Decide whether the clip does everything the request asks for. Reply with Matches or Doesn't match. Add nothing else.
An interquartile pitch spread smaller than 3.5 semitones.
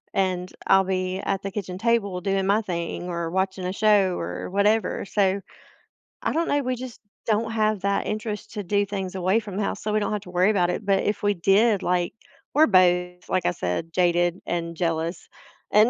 Matches